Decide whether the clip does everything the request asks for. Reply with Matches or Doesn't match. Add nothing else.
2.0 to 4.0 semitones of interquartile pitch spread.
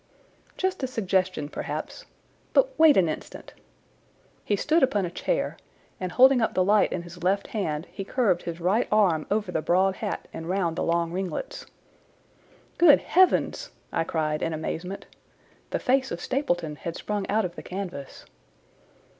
Doesn't match